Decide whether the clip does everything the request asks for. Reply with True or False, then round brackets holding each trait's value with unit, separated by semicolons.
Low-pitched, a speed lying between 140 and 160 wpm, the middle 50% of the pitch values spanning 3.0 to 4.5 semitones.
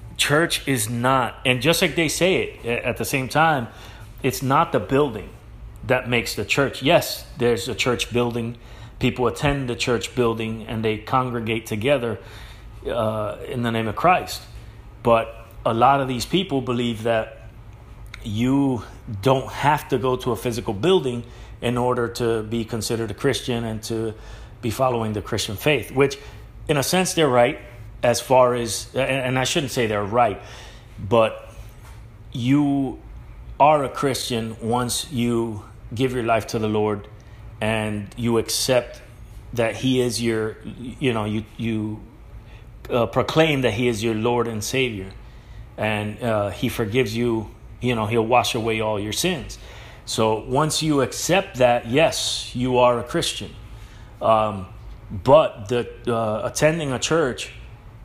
False (115 Hz; 155 wpm; 2.5 semitones)